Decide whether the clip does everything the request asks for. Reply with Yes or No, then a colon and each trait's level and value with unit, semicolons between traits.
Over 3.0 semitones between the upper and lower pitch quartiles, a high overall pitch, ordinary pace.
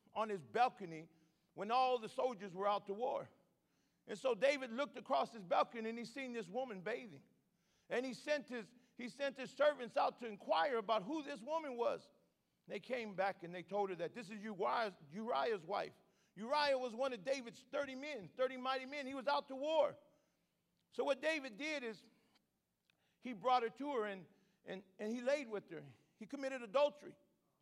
Yes: average, 4.9 semitones; high, 245 Hz; average, 190 wpm